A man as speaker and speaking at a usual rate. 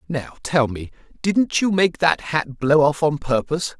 Yes: male; average, 175 wpm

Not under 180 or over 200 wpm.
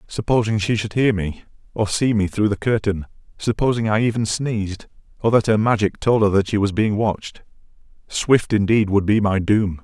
Yes: average, 190 wpm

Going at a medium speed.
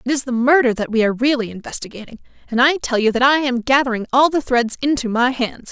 No: fast, 240 wpm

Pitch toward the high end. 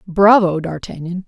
No: medium, 180 Hz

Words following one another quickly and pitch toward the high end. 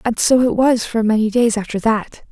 Yes: fast, 235 wpm; high, 225 Hz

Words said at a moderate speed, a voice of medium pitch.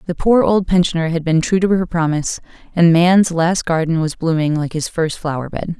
No: fast, 215 wpm; medium, 170 Hz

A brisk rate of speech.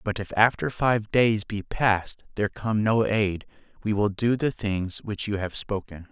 No: average, 195 wpm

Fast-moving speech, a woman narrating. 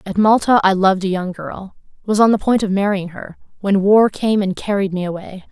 Yes: fast, 230 wpm; female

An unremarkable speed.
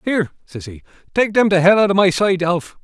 No: fast, 255 wpm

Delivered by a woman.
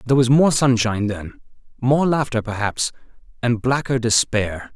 No: male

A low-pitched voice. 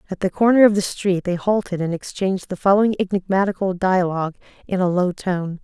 No: medium, 185 Hz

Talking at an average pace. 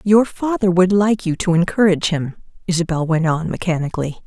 Yes: average, 170 wpm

